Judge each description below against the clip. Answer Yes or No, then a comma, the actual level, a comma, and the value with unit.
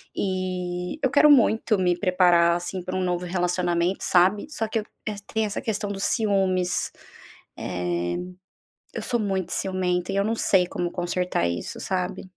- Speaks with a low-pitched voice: No, medium, 185 Hz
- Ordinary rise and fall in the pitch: No, narrow, 2.2 semitones